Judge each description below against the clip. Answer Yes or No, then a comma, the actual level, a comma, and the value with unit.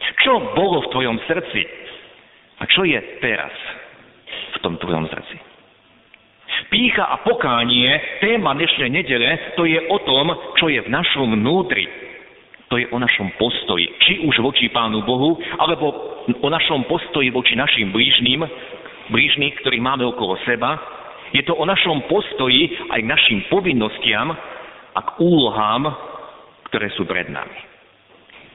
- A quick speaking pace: No, average, 140 wpm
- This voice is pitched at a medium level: Yes, medium, 165 Hz